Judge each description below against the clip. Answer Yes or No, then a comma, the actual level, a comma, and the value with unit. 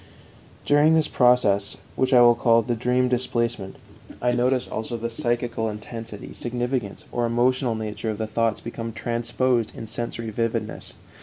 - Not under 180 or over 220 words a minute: No, average, 150 wpm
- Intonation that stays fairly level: Yes, narrow, 1.7 semitones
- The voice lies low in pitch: Yes, low, 120 Hz